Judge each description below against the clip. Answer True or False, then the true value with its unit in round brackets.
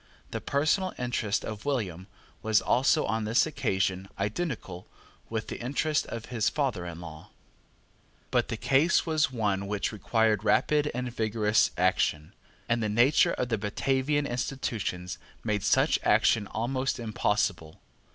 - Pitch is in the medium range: False (110 Hz)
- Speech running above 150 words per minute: False (140 wpm)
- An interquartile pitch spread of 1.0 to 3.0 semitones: False (4.7 semitones)